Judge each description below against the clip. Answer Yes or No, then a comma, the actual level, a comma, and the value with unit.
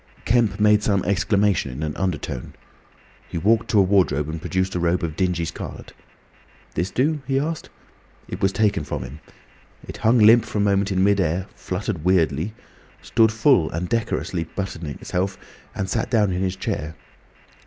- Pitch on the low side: Yes, very low, 95 Hz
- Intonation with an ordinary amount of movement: Yes, average, 3.8 semitones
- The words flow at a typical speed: Yes, average, 175 wpm